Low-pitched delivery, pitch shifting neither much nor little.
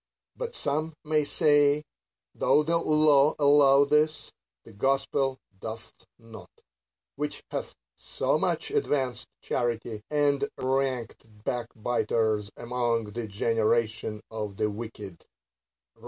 Yes: low, 125 Hz; average, 4.6 semitones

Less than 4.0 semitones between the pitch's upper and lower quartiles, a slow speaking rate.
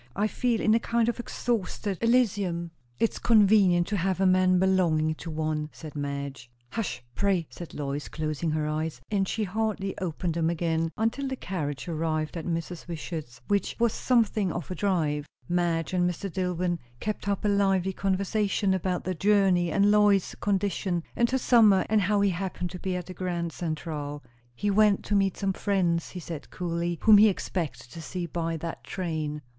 No: average, 3.6 semitones; average, 185 wpm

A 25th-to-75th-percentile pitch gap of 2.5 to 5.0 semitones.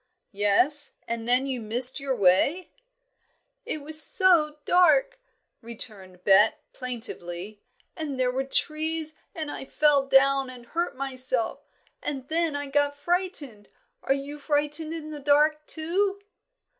Yes: average, 3.8 semitones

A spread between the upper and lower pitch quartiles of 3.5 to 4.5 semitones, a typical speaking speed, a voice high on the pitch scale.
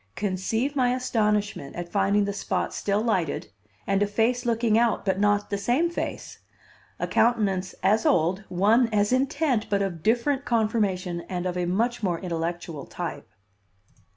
Yes: average, 4.0 semitones; average, 155 wpm; high, 205 Hz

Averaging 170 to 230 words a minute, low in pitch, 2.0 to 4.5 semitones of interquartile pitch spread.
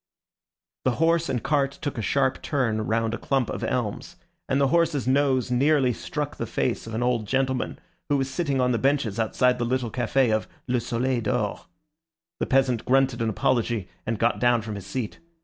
Yes: average, 195 wpm; low, 125 Hz; average, 2.8 semitones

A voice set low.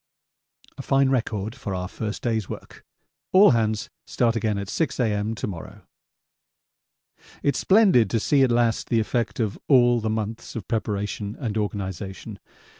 Yes: low, 110 Hz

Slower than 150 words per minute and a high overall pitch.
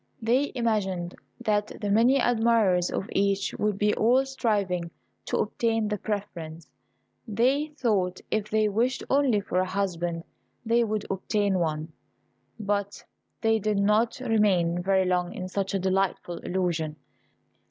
Yes: average, 140 wpm; high, 205 Hz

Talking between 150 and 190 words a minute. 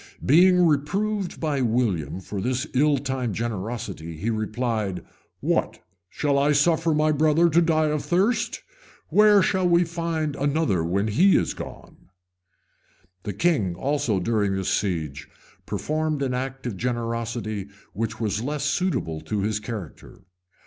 No: average, 140 wpm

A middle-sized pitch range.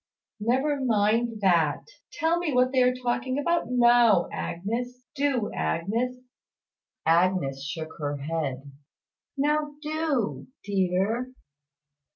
No: wide, 7.2 semitones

